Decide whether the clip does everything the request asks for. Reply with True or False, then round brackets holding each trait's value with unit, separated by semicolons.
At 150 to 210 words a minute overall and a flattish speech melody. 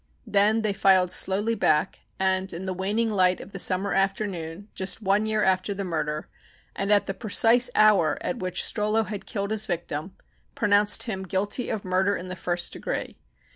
True (180 wpm; 2.3 semitones)